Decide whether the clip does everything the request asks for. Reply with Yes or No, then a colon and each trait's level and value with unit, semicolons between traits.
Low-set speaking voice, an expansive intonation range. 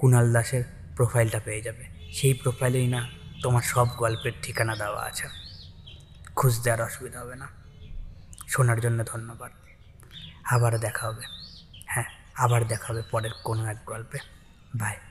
No: low, 115 Hz; average, 3.0 semitones